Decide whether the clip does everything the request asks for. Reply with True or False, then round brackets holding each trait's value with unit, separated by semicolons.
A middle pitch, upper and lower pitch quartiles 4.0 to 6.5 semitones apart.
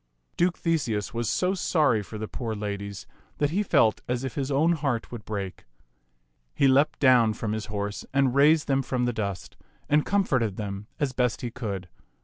False (125 Hz; 5.1 semitones)